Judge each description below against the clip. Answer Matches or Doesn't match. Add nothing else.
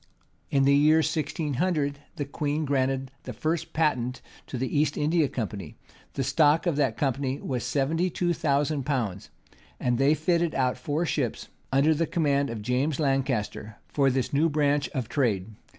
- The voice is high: Doesn't match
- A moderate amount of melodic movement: Matches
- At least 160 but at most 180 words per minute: Matches